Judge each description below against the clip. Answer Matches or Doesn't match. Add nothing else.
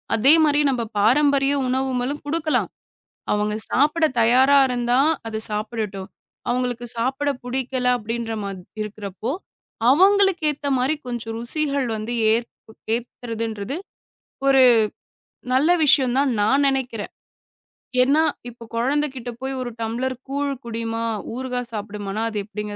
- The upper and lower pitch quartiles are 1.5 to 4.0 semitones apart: Matches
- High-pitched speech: Matches